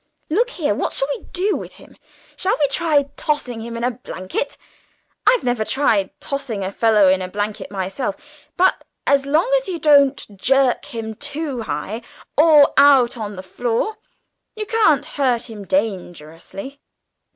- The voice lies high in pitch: Yes, very high, 255 Hz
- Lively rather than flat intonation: Yes, wide, 5.8 semitones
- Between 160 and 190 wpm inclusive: No, average, 150 wpm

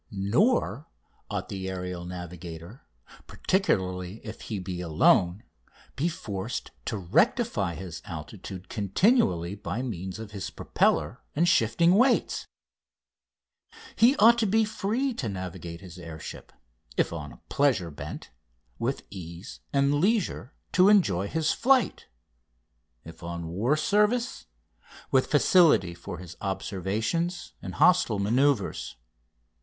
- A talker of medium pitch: No, low, 105 Hz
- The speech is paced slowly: Yes, slow, 120 wpm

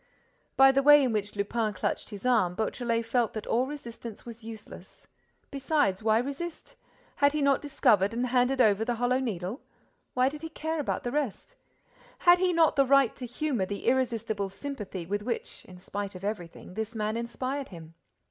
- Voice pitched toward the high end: Yes, high, 235 Hz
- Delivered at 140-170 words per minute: No, average, 185 wpm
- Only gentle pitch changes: No, average, 4.7 semitones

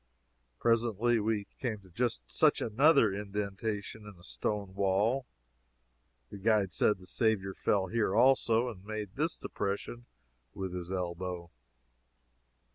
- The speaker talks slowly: Yes, slow, 125 wpm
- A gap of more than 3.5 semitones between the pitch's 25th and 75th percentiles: No, average, 3.2 semitones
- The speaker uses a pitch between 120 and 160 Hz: No, low, 105 Hz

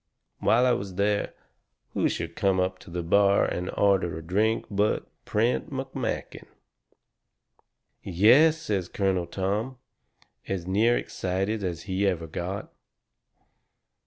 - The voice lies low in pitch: Yes, low, 100 Hz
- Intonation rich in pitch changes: No, average, 3.1 semitones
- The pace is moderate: No, slow, 125 wpm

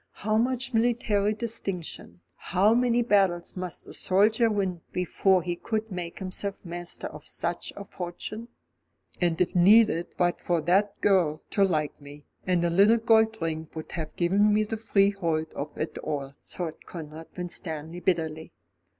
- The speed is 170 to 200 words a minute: No, average, 155 wpm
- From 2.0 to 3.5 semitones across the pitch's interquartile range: No, average, 4.0 semitones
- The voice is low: No, medium, 185 Hz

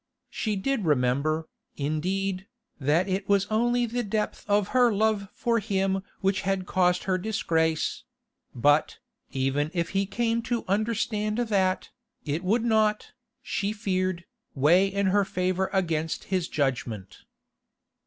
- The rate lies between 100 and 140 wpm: Yes, slow, 135 wpm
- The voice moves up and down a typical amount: Yes, average, 4.6 semitones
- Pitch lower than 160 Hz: No, high, 190 Hz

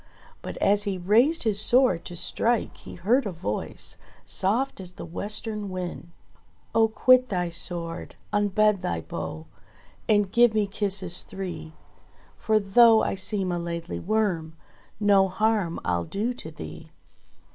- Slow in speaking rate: No, average, 145 wpm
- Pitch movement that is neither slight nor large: Yes, average, 3.9 semitones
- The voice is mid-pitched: No, high, 195 Hz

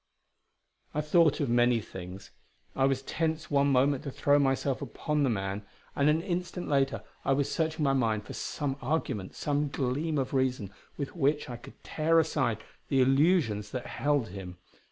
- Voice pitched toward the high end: No, low, 135 Hz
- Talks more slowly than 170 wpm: No, average, 175 wpm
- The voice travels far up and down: No, average, 3.6 semitones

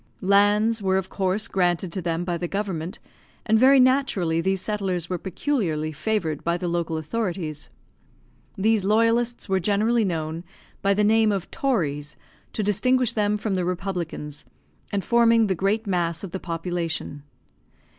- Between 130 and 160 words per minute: Yes, average, 155 wpm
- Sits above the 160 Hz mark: Yes, high, 190 Hz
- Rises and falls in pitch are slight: No, average, 4.1 semitones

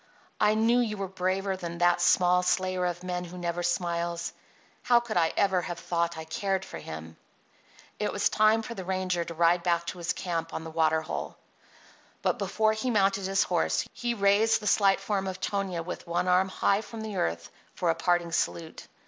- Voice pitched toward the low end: No, medium, 180 Hz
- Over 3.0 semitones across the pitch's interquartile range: No, average, 2.7 semitones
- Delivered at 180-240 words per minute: Yes, average, 200 wpm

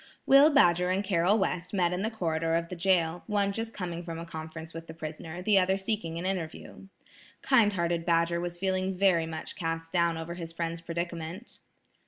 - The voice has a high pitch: No, medium, 175 Hz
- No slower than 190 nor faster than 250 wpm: Yes, average, 195 wpm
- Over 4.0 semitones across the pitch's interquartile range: No, narrow, 2.5 semitones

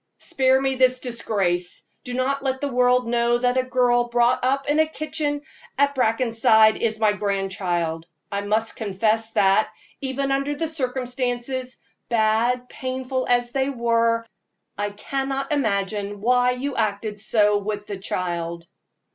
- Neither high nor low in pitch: No, high, 240 Hz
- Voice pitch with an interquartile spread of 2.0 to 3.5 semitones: No, average, 3.9 semitones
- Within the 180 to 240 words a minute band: No, average, 145 wpm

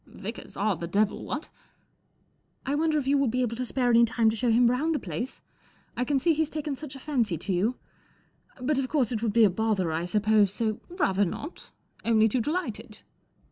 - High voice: Yes, high, 235 Hz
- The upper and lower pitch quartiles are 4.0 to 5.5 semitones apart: Yes, average, 4.7 semitones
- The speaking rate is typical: No, fast, 235 wpm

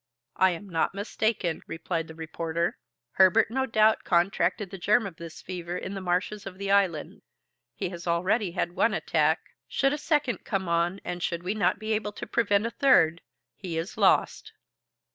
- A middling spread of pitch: Yes, average, 3.7 semitones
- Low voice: No, high, 190 Hz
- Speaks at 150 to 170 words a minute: No, average, 180 wpm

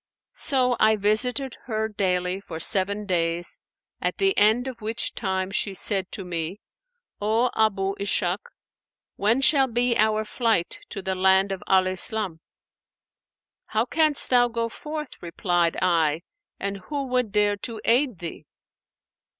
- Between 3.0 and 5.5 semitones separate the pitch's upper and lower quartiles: Yes, average, 4.2 semitones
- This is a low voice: No, high, 210 Hz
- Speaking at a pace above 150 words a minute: No, average, 140 wpm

